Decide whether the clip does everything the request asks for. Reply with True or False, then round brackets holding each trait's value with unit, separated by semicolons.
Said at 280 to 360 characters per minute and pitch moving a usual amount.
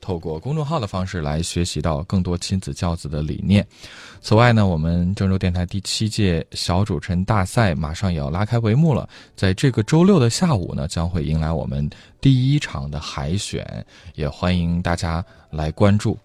True (285 characters per minute; 4.7 semitones)